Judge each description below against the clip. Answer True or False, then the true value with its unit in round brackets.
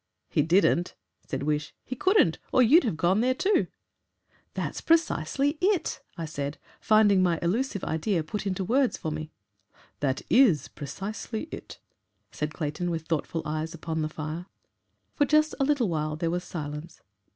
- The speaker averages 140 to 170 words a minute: True (160 wpm)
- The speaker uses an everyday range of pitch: False (7.8 semitones)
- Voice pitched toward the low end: False (175 Hz)